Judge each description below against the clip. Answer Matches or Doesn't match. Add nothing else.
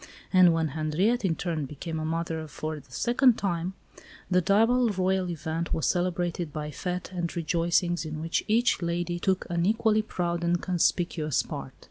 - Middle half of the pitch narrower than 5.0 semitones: Matches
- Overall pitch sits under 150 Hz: Doesn't match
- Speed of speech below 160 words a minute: Doesn't match